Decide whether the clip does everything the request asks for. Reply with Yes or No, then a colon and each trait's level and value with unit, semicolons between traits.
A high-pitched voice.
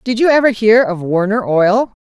Yes: high, 220 Hz